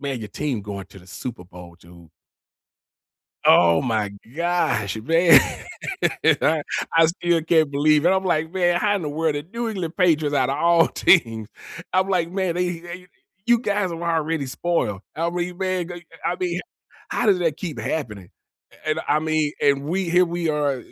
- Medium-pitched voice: Yes, medium, 165 Hz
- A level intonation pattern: No, average, 4.2 semitones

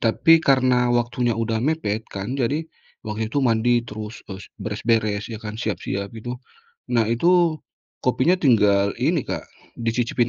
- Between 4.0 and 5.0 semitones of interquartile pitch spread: No, average, 2.9 semitones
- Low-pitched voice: Yes, low, 115 Hz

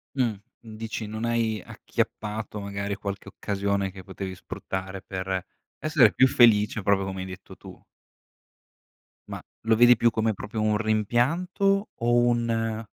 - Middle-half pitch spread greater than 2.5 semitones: Yes, average, 2.9 semitones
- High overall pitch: No, low, 110 Hz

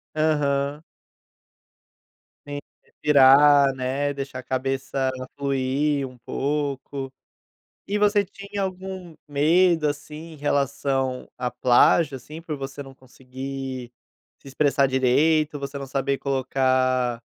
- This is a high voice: No, medium, 140 Hz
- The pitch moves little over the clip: Yes, narrow, 2.2 semitones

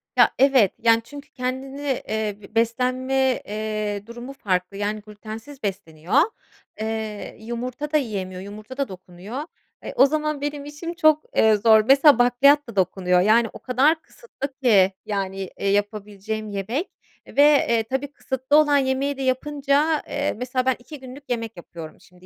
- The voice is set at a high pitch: Yes, high, 240 Hz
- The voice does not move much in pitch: No, average, 5.0 semitones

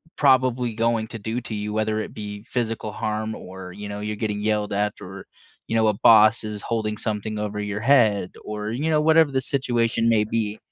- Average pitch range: No, narrow, 1.9 semitones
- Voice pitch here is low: Yes, low, 110 Hz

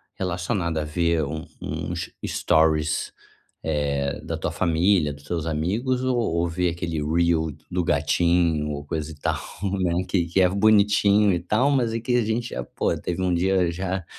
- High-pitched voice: No, very low, 85 Hz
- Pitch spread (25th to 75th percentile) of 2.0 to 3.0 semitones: No, average, 3.7 semitones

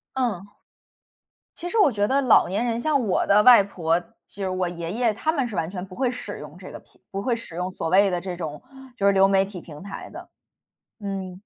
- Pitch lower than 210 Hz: Yes, high, 195 Hz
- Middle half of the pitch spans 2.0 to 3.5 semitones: No, average, 4.6 semitones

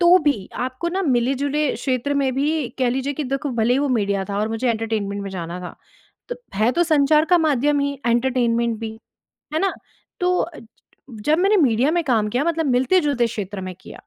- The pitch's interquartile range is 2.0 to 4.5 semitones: No, average, 5.1 semitones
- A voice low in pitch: No, very high, 260 Hz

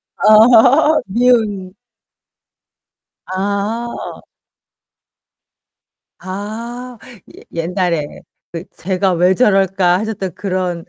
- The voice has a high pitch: Yes, high, 195 Hz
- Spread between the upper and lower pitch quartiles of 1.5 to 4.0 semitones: Yes, average, 3.6 semitones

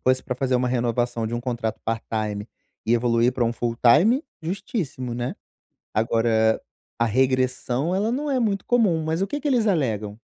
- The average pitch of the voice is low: Yes, low, 125 Hz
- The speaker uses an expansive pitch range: Yes, wide, 6.5 semitones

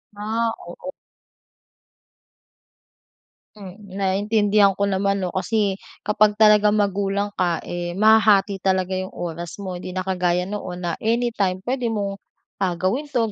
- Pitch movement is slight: Yes, narrow, 2.2 semitones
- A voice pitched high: Yes, high, 200 Hz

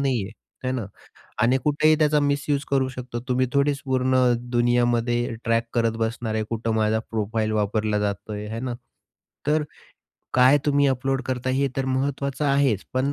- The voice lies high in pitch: No, low, 125 Hz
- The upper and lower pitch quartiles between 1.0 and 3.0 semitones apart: No, average, 3.4 semitones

